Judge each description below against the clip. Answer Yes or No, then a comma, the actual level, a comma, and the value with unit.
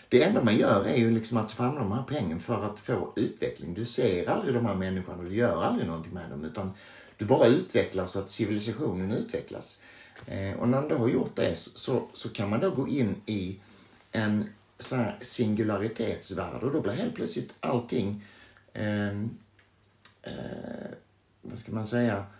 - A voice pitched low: Yes, low, 105 Hz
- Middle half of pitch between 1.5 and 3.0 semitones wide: Yes, narrow, 2.5 semitones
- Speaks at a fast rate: No, average, 175 wpm